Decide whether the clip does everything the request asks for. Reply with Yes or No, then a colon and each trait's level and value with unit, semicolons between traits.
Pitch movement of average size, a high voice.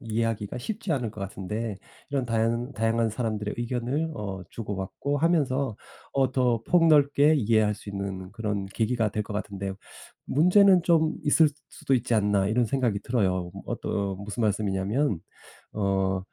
No: average, 5.0 semitones; low, 115 Hz